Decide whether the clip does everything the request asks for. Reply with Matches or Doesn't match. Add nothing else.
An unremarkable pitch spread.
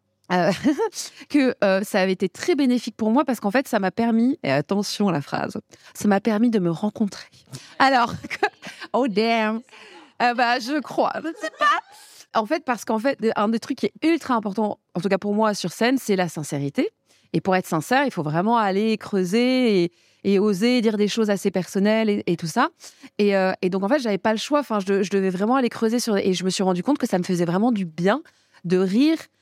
Matches